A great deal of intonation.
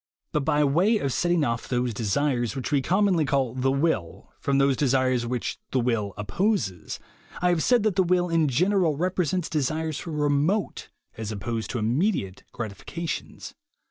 Yes: wide, 6.2 semitones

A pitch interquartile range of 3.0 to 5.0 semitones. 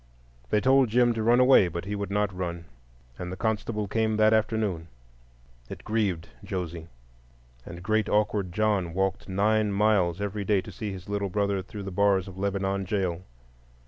No: narrow, 2.6 semitones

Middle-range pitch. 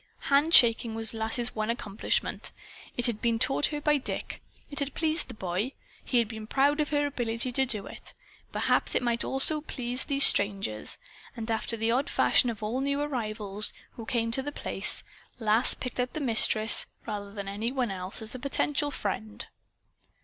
No: high, 235 Hz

